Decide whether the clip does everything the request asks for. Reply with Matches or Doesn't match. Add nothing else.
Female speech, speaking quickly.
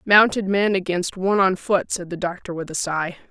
Matches